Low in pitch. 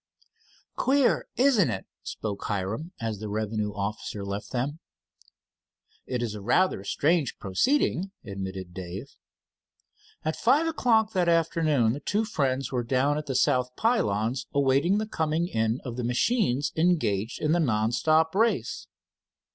Yes: low, 130 Hz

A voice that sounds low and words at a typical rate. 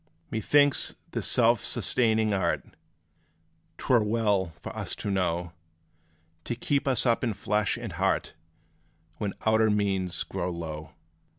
No: low, 105 Hz; slow, 130 wpm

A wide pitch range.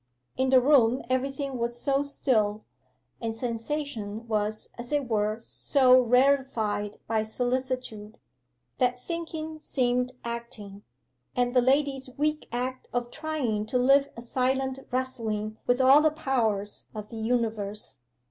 No: average, 3.3 semitones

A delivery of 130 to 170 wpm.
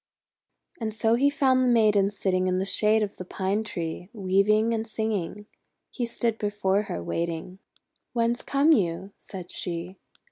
Yes: average, 155 wpm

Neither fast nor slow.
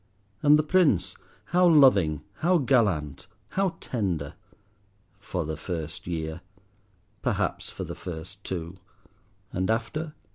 No: slow, 110 wpm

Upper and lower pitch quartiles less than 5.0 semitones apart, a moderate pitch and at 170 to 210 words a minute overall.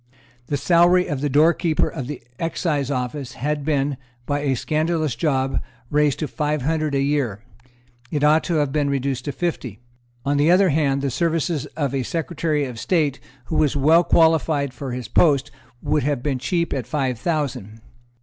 Yes: average, 2.8 semitones; medium, 145 Hz; average, 180 wpm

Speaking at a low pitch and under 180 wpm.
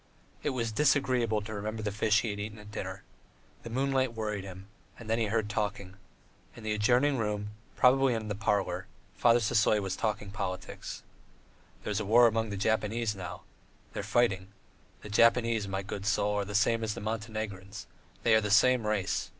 No: low, 110 Hz; average, 185 wpm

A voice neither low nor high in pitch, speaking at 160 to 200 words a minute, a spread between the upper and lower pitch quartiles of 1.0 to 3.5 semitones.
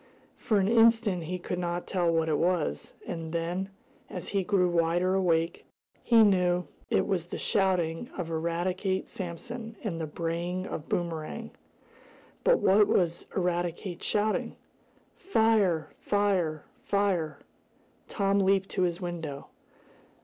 No: medium, 180 Hz; slow, 135 wpm; average, 2.9 semitones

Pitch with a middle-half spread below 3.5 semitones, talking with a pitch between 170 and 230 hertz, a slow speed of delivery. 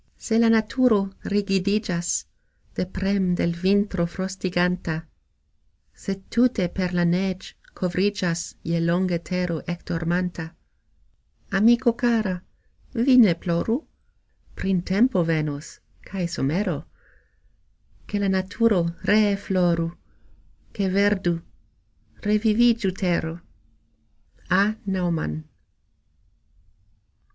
Yes: average, 3.1 semitones; medium, 185 Hz; slow, 90 wpm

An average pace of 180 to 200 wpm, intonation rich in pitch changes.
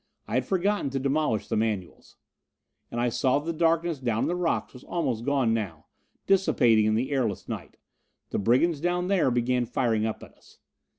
Yes: average, 190 wpm; wide, 6.7 semitones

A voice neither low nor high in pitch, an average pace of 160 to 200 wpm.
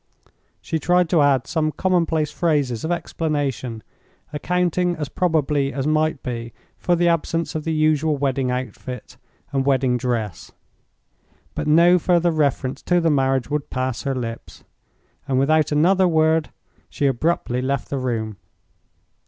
No: medium, 150 Hz; average, 145 wpm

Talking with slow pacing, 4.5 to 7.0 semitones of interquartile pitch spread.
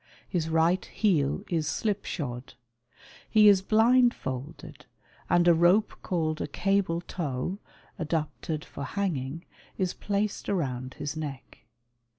Yes: slow, 120 wpm; average, 5.1 semitones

